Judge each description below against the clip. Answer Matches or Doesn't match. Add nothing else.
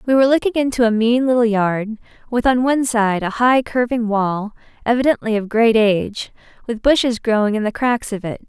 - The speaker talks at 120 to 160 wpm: Doesn't match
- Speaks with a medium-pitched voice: Doesn't match